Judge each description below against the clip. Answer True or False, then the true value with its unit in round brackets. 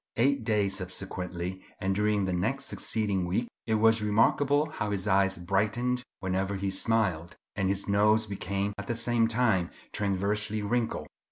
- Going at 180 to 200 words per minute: False (155 wpm)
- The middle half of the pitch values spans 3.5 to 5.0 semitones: False (2.8 semitones)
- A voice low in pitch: True (100 Hz)